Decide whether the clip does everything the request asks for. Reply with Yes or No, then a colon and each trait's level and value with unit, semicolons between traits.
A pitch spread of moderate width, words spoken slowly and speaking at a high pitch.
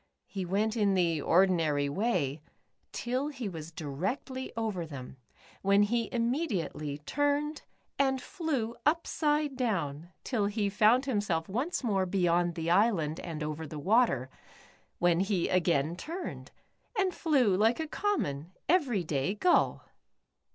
No: wide, 7.5 semitones; slow, 130 wpm; high, 200 Hz